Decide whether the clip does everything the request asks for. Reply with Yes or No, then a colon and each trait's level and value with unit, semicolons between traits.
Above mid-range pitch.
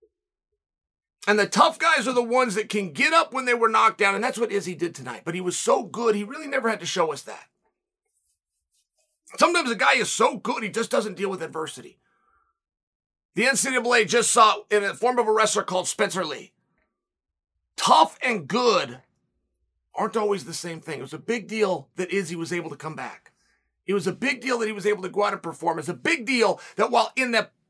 Yes: high, 210 Hz